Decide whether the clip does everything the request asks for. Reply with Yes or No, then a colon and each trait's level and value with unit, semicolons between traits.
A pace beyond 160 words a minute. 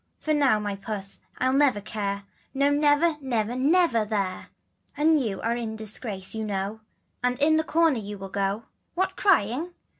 Yes: average, 170 wpm